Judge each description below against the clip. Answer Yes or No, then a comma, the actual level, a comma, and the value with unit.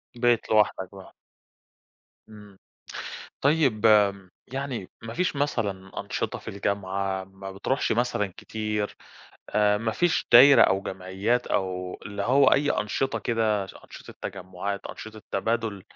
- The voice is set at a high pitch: No, low, 105 Hz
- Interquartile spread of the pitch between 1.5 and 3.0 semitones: No, average, 3.5 semitones